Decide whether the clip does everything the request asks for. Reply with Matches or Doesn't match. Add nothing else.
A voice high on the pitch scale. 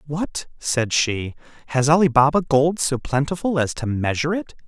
Doesn't match